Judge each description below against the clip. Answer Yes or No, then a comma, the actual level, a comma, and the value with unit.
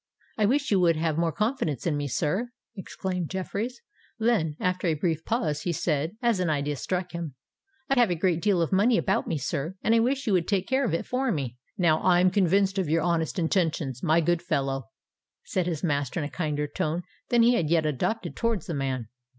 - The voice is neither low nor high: Yes, medium, 175 Hz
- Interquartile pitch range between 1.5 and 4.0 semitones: No, average, 4.6 semitones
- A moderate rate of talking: No, fast, 215 wpm